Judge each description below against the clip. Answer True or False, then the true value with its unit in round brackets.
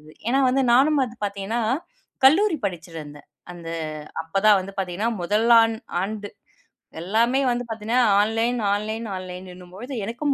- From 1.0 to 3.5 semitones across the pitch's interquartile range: False (4.5 semitones)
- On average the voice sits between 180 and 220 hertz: True (215 Hz)